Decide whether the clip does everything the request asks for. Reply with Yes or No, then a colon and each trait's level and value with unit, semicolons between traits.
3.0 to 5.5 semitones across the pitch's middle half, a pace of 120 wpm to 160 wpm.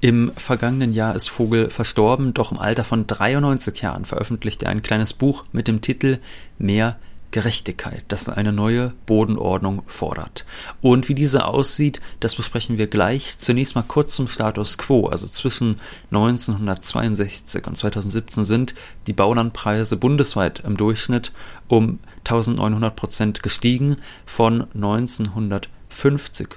No: narrow, 2.6 semitones; average, 130 wpm